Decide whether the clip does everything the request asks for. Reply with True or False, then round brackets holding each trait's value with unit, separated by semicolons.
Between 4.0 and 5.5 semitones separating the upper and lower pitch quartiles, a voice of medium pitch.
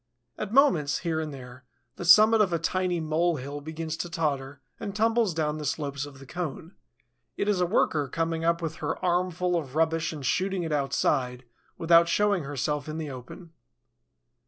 False (3.5 semitones; 160 Hz)